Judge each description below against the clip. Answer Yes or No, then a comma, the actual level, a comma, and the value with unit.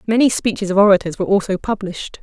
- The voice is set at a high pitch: Yes, high, 200 Hz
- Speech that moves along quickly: No, average, 190 wpm